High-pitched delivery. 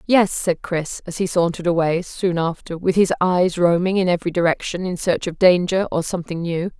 No: medium, 175 Hz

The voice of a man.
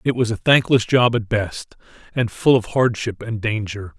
Yes: male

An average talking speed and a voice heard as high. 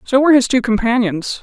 No: fast, 210 wpm; high, 240 Hz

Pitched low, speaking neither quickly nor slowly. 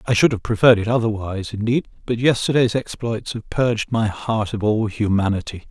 Yes: low, 110 Hz; average, 180 wpm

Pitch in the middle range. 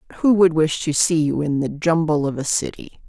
Yes: medium, 160 Hz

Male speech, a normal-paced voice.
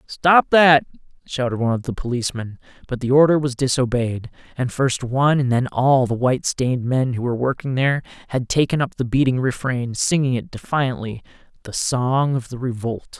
Yes: male; average, 175 wpm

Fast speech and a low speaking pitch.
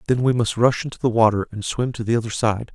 Yes: fast, 285 wpm; low, 115 Hz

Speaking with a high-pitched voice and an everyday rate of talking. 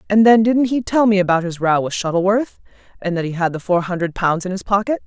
No: high, 195 Hz; fast, 260 wpm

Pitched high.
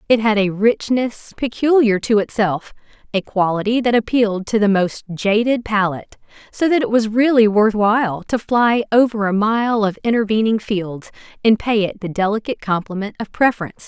Yes: high, 215 Hz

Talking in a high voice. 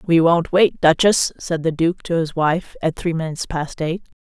No: medium, 165 Hz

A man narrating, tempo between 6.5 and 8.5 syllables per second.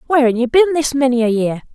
No: female; 7.4 syllables/s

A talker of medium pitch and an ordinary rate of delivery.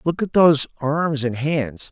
Yes: medium, 145 Hz; average, 190 wpm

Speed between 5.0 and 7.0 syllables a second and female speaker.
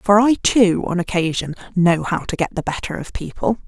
Yes: 5.1 syllables/s; female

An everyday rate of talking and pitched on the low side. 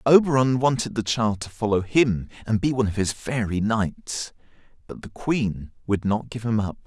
Yes: average, 190 wpm; low, 115 Hz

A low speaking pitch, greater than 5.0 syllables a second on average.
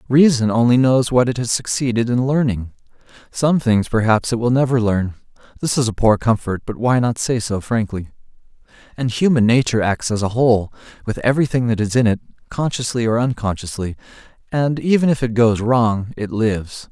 Yes: low, 120 Hz; 5.5 syllables/s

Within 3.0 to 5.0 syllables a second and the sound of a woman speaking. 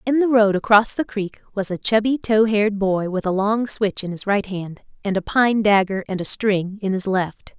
Yes: 4.8 syllables/s; female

